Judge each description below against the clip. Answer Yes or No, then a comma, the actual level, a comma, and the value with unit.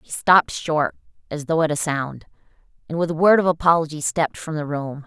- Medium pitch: Yes, medium, 155 Hz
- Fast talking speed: Yes, fast, 215 wpm